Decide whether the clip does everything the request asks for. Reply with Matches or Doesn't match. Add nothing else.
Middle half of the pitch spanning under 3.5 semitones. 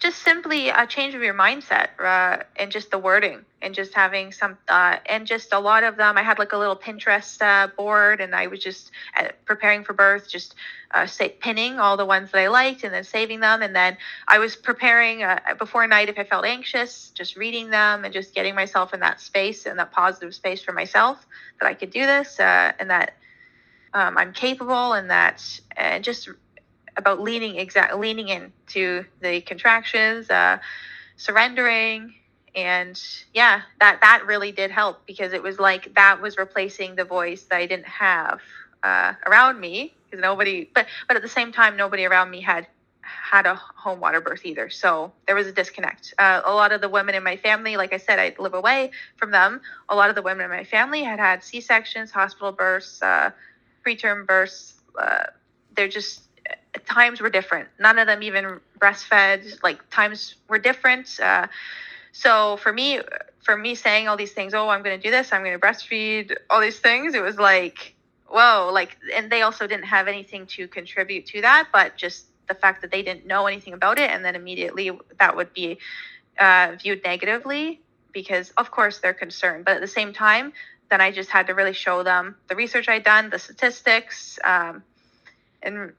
Matches